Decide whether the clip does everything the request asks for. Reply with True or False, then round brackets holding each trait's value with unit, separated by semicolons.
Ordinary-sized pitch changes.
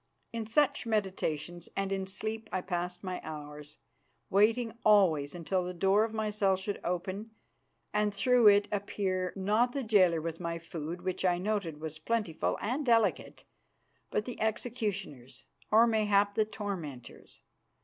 True (3.8 semitones)